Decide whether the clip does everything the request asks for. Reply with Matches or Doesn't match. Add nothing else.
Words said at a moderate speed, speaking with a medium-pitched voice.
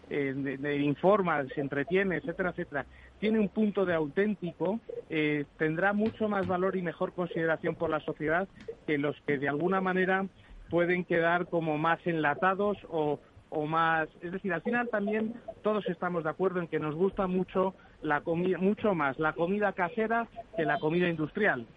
Matches